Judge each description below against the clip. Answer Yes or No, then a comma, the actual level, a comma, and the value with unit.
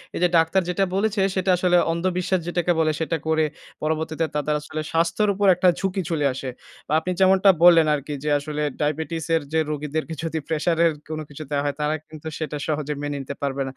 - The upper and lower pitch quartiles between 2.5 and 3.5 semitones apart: Yes, average, 2.8 semitones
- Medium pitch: Yes, medium, 160 Hz